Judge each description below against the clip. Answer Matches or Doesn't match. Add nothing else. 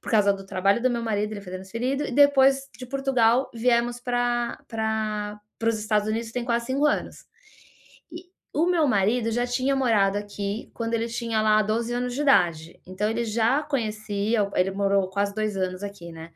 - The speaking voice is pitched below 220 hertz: Doesn't match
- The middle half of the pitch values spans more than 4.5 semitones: Doesn't match